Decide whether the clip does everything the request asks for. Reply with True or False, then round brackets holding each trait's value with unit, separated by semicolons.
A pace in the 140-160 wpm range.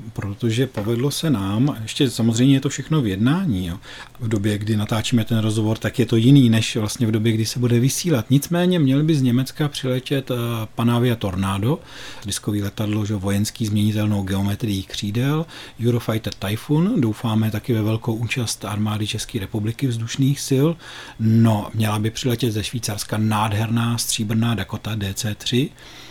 True (155 wpm)